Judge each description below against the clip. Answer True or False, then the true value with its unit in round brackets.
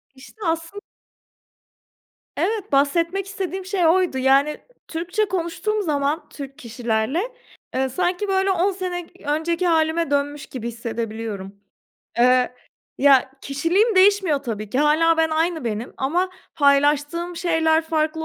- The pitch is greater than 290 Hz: True (320 Hz)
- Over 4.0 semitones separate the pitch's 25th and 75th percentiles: True (4.7 semitones)